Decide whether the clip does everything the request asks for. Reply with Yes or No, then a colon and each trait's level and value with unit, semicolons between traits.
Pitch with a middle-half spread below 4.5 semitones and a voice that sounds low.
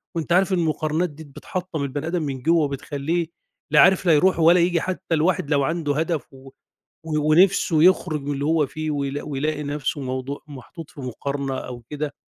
No: average, 2.9 semitones; medium, 150 Hz